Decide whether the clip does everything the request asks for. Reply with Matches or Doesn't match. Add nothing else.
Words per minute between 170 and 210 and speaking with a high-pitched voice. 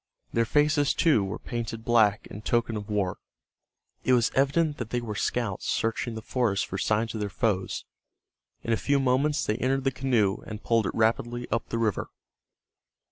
Doesn't match